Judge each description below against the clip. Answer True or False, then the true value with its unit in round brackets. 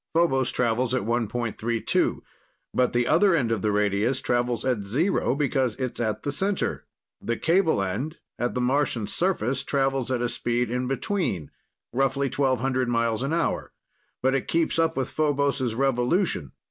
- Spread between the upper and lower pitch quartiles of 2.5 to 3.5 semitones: True (3.2 semitones)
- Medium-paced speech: True (160 wpm)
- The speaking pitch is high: False (130 Hz)